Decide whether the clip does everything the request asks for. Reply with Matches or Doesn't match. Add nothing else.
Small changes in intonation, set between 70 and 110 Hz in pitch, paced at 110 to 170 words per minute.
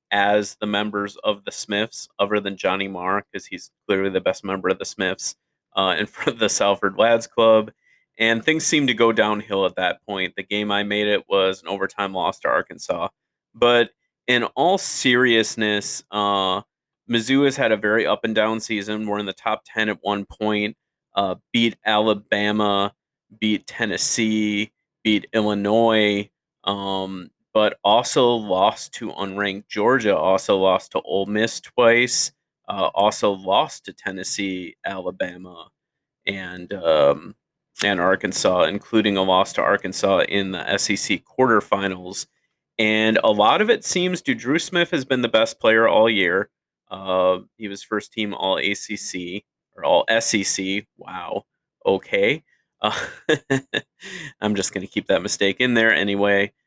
Matches